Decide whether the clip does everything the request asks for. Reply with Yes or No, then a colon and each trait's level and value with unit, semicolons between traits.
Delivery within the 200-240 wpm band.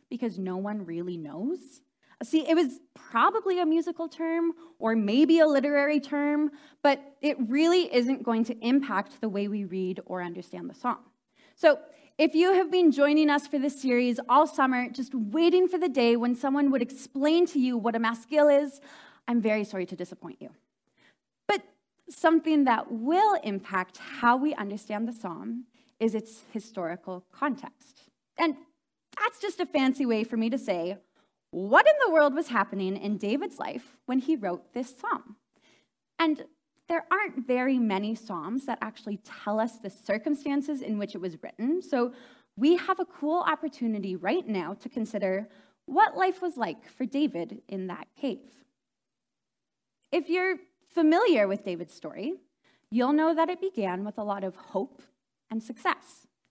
No: average, 165 wpm